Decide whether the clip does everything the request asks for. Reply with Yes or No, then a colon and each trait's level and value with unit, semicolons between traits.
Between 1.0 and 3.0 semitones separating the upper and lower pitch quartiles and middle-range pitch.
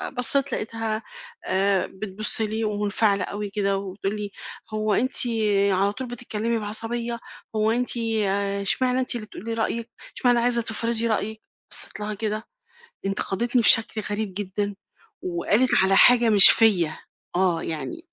No: average, 2.7 semitones; high, 215 Hz